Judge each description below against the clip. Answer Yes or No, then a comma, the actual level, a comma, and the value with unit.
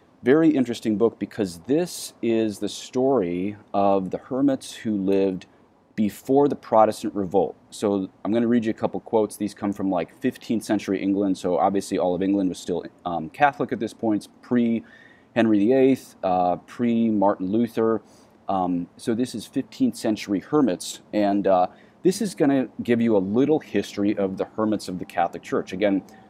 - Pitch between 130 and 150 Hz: No, low, 105 Hz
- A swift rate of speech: No, average, 180 wpm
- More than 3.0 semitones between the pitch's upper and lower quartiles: Yes, average, 3.4 semitones